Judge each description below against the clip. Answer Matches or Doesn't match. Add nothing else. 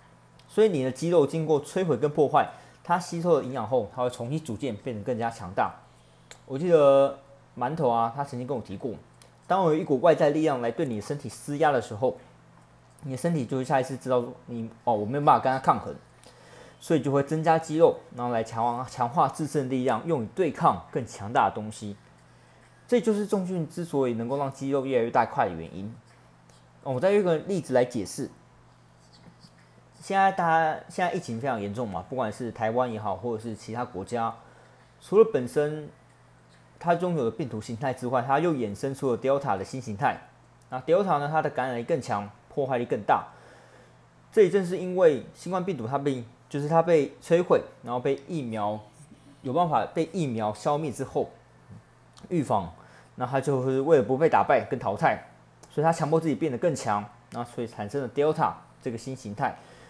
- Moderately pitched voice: Doesn't match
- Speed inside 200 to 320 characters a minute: Matches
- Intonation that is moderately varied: Doesn't match